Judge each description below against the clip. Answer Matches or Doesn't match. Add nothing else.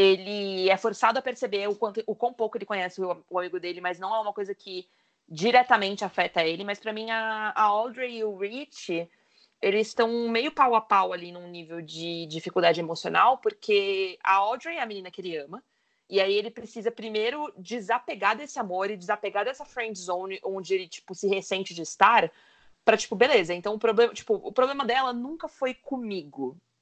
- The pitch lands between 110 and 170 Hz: Doesn't match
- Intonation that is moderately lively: Matches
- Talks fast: Matches